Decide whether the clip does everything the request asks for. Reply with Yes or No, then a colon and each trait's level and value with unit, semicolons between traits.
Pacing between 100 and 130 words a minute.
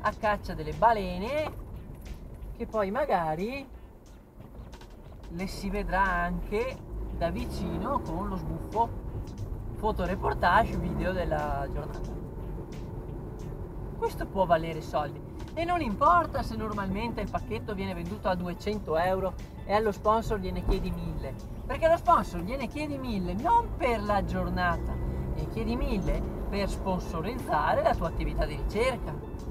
Yes: average, 125 wpm